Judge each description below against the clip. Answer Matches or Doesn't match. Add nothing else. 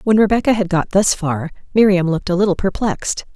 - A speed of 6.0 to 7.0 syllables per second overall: Matches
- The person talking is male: Doesn't match